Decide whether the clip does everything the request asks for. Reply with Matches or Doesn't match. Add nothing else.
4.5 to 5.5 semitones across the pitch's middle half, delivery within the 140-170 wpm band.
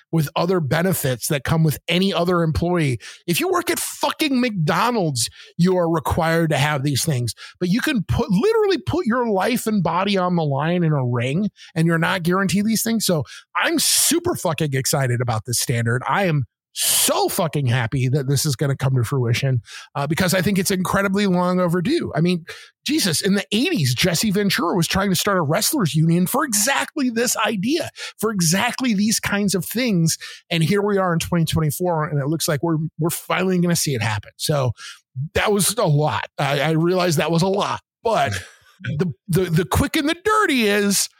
Doesn't match